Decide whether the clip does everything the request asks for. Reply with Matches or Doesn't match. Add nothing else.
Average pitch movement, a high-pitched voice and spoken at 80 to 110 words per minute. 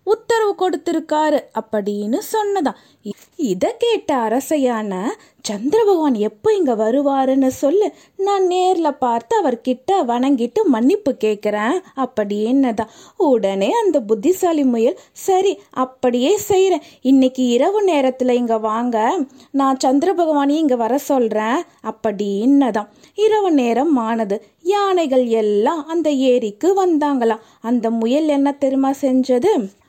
Doesn't match